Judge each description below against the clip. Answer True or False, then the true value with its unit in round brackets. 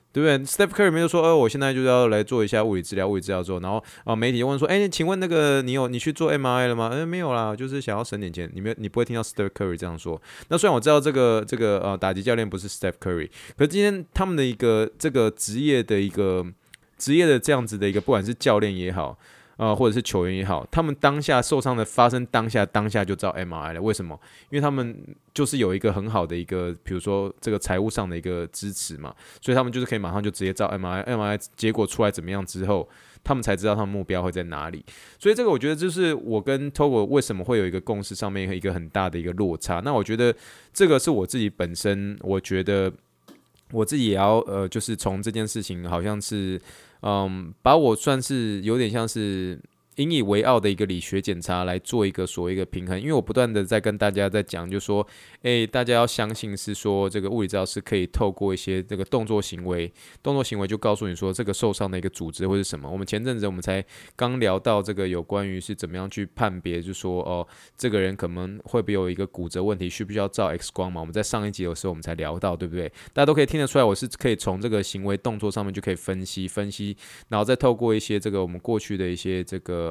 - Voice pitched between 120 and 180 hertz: False (105 Hz)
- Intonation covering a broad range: False (4.2 semitones)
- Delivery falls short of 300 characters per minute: False (395 characters per minute)